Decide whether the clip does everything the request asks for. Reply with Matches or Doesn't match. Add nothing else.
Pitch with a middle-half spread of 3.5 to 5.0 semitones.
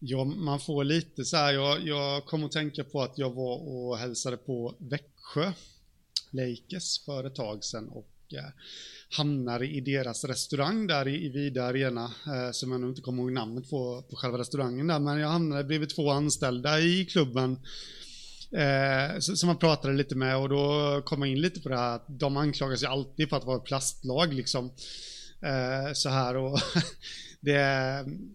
Doesn't match